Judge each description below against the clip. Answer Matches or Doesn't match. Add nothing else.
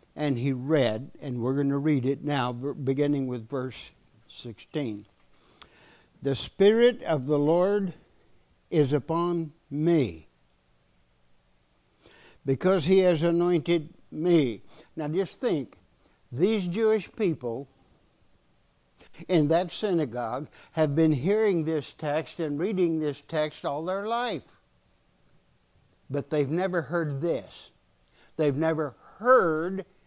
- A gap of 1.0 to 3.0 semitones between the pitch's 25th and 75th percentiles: Doesn't match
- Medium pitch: Matches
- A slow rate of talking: Matches